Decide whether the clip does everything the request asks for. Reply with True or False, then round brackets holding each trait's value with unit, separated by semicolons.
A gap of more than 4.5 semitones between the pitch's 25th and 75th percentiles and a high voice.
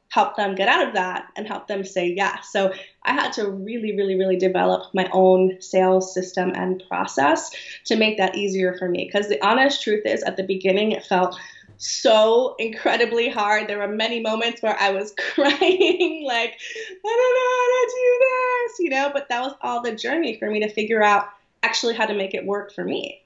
True (5.2 semitones; 215 Hz)